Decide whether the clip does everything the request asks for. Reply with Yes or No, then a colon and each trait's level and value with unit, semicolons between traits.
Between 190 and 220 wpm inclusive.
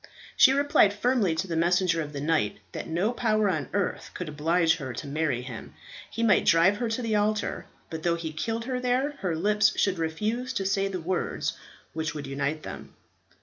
Yes: average, 200 wpm